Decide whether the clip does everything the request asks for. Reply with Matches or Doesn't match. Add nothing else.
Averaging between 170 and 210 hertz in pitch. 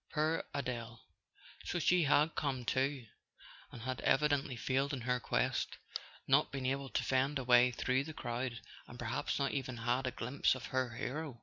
Doesn't match